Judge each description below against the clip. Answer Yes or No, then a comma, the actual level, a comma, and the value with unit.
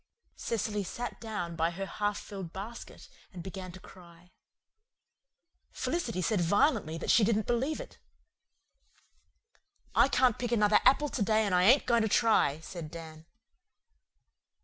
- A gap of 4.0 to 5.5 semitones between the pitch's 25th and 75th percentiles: Yes, average, 4.7 semitones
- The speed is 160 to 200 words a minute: No, average, 145 wpm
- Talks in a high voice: Yes, high, 205 Hz